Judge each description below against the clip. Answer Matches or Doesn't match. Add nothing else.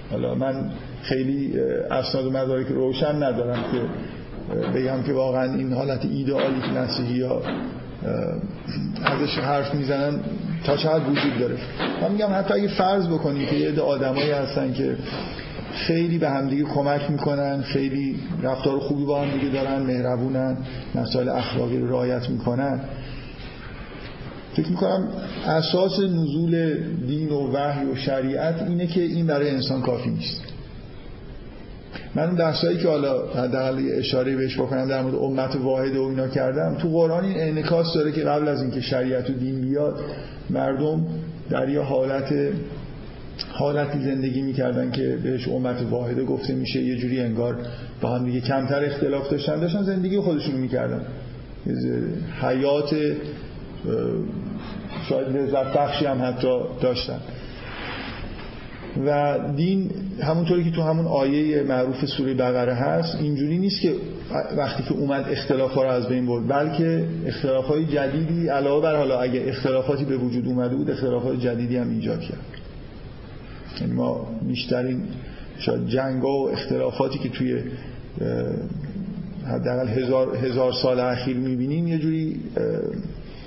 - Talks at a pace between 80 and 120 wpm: Doesn't match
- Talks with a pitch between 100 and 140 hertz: Matches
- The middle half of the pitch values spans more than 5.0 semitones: Doesn't match